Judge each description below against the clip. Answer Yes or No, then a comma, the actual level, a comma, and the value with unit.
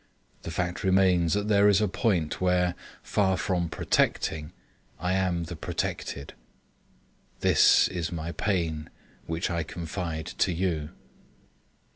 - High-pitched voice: No, very low, 90 Hz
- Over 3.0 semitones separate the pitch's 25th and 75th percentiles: No, narrow, 2.6 semitones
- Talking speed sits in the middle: No, slow, 125 wpm